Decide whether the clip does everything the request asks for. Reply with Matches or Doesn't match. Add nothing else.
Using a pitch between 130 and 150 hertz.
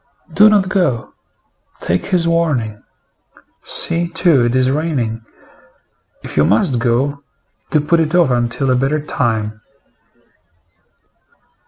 Matches